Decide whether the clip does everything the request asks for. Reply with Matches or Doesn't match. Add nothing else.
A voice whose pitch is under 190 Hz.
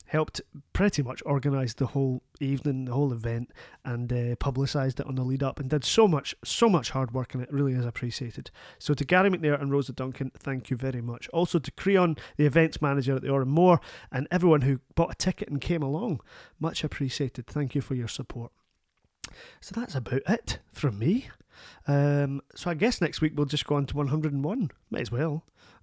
Matches